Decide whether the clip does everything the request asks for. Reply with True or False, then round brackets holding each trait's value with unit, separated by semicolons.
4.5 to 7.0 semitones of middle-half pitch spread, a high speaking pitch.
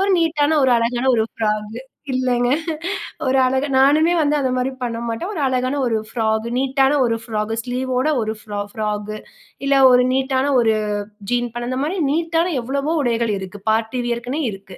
False (3.5 semitones; 250 Hz)